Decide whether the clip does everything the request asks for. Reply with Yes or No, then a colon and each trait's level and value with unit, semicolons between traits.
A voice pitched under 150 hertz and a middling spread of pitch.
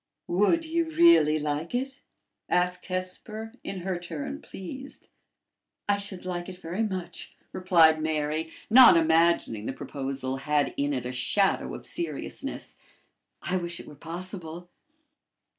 No: medium, 175 Hz; average, 4.6 semitones